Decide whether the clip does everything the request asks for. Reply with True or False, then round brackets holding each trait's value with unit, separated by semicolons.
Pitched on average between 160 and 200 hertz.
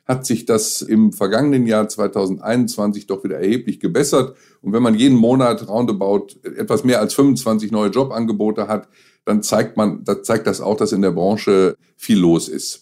False (110 Hz)